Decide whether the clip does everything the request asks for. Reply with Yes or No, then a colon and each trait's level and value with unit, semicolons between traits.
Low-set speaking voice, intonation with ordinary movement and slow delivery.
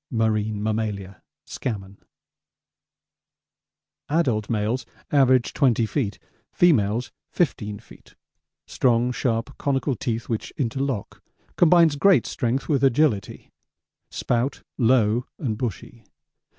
Yes: low, 120 Hz; average, 4.0 semitones; slow, 95 wpm